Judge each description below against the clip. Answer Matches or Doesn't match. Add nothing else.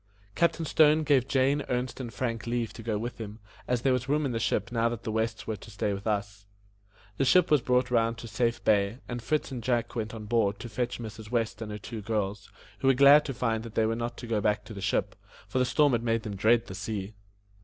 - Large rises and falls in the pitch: Doesn't match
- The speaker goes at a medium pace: Doesn't match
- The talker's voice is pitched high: Doesn't match